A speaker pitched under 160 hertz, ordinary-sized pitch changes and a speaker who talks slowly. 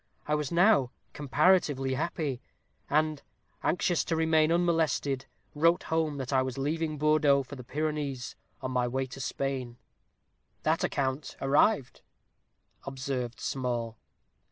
Yes: medium, 140 Hz; average, 3.2 semitones; slow, 125 wpm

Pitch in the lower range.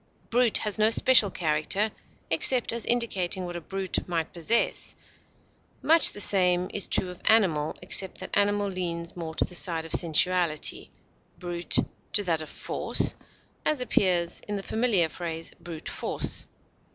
No: medium, 185 Hz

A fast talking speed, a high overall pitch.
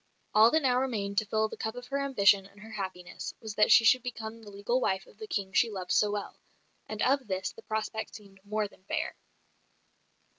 Yes: fast, 220 wpm; high, 215 Hz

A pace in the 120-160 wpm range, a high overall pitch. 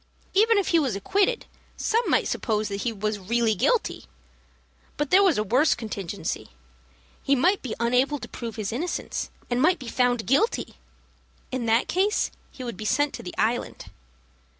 No: average, 175 wpm; very high, 250 Hz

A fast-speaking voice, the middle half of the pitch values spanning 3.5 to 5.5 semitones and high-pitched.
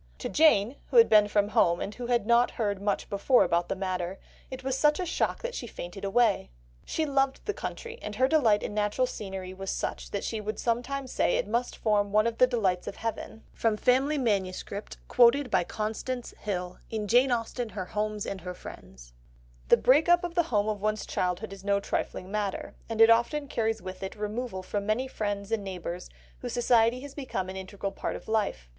Yes: fast, 210 wpm; average, 4.1 semitones; high, 215 Hz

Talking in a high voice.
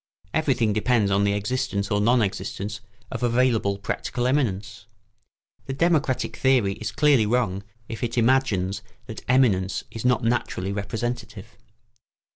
No: low, 115 Hz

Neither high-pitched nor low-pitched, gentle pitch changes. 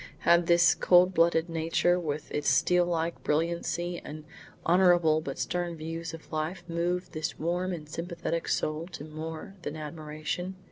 Yes: medium, 165 Hz; narrow, 1.9 semitones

